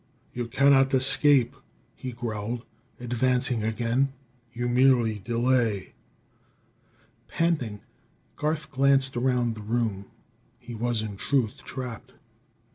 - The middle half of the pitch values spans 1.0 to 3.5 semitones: Yes, narrow, 2.5 semitones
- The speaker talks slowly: Yes, slow, 100 wpm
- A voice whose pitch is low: Yes, low, 120 Hz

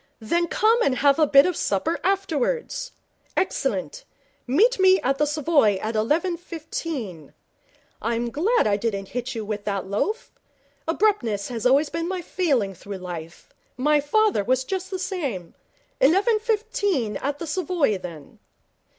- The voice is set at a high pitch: Yes, very high, 290 Hz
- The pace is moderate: Yes, average, 145 wpm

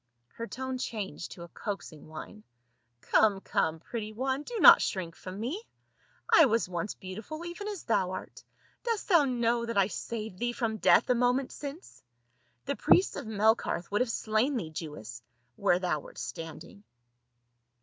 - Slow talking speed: No, average, 170 wpm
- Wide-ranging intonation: Yes, wide, 5.7 semitones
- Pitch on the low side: No, high, 220 Hz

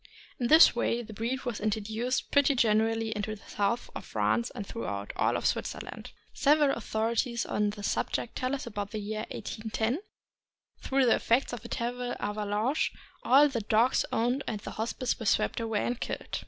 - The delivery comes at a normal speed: Yes, average, 180 wpm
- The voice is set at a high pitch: Yes, high, 230 Hz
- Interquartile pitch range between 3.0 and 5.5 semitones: No, narrow, 2.6 semitones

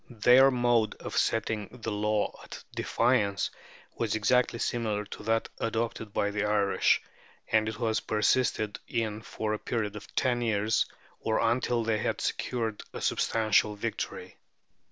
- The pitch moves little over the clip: Yes, narrow, 1.8 semitones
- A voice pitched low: Yes, low, 110 Hz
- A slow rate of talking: No, average, 145 wpm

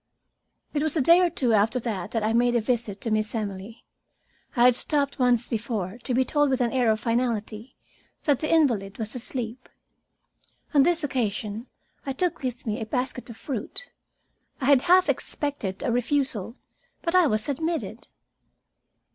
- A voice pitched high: Yes, high, 245 Hz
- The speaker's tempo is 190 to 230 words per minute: No, average, 170 wpm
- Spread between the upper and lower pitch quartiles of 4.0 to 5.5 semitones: Yes, average, 4.3 semitones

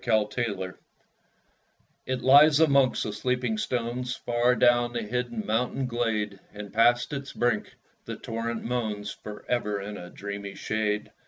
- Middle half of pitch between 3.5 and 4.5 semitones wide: No, average, 2.9 semitones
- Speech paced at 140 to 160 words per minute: Yes, average, 145 wpm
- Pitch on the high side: No, low, 115 Hz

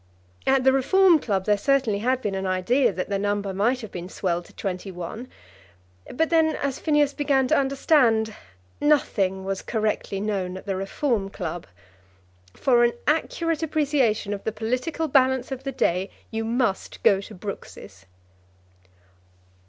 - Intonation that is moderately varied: No, wide, 5.7 semitones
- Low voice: No, high, 225 Hz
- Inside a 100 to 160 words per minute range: Yes, average, 155 wpm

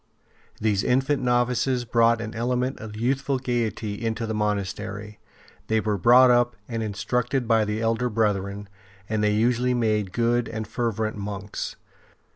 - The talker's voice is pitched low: Yes, low, 115 Hz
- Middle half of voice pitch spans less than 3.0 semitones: Yes, narrow, 2.5 semitones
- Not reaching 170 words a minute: Yes, average, 150 wpm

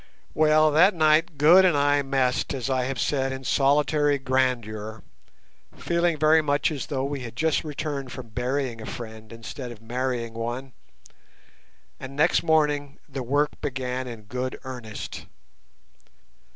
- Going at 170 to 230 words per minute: No, average, 145 wpm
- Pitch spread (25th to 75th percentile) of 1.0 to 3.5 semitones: Yes, average, 3.2 semitones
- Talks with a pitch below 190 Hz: Yes, low, 135 Hz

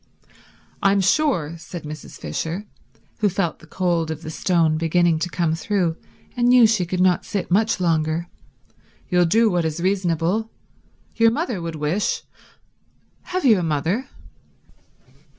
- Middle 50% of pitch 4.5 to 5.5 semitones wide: No, average, 4.1 semitones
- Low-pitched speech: No, medium, 175 Hz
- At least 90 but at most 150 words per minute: Yes, average, 140 wpm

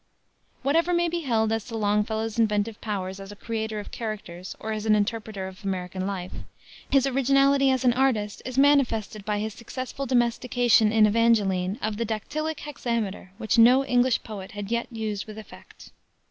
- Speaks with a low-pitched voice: No, high, 220 Hz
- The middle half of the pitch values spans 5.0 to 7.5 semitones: No, average, 3.4 semitones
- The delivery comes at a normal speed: Yes, average, 170 wpm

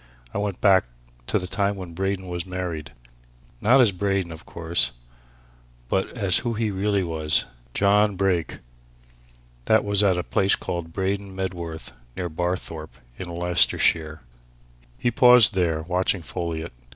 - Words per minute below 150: Yes, average, 140 wpm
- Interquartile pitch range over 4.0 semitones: No, average, 2.9 semitones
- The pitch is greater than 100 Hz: No, very low, 95 Hz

